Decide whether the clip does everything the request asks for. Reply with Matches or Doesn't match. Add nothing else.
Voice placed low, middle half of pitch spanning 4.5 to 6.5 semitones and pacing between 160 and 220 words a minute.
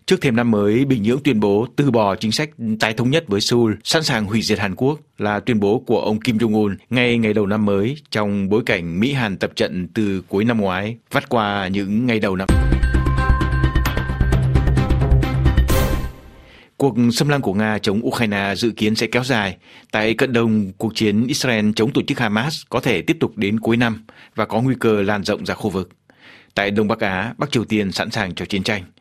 Doesn't match